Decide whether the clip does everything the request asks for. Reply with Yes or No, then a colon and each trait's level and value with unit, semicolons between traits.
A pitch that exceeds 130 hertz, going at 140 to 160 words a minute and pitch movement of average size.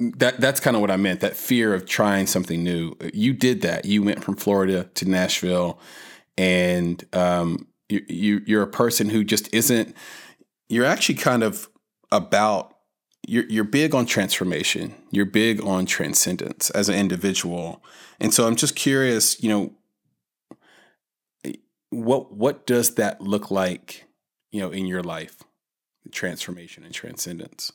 No: low, 100 Hz; average, 150 wpm; average, 3.7 semitones